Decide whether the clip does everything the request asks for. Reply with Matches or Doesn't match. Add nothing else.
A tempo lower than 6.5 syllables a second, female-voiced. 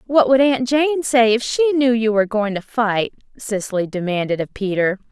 Matches